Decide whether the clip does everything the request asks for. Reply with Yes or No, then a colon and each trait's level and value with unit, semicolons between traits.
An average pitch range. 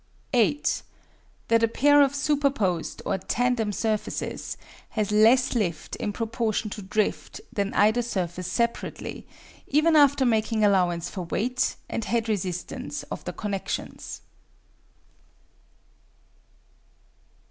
Yes: average, 3.7 semitones